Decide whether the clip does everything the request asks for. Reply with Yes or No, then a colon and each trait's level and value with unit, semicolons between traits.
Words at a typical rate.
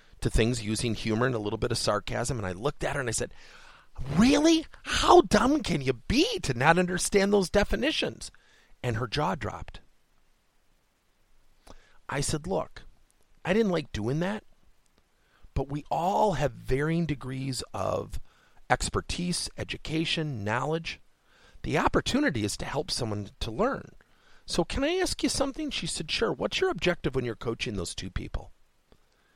Yes: average, 155 wpm